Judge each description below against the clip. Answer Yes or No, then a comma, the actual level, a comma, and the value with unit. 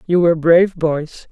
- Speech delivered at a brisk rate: No, average, 185 wpm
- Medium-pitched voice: Yes, medium, 165 Hz